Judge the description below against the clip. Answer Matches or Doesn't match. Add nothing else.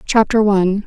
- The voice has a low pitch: Doesn't match